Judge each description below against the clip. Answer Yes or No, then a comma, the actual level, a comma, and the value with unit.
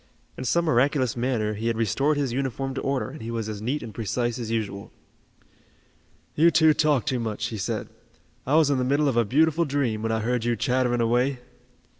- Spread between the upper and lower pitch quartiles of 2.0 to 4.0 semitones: Yes, average, 3.5 semitones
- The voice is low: Yes, low, 125 Hz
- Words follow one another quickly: Yes, fast, 210 wpm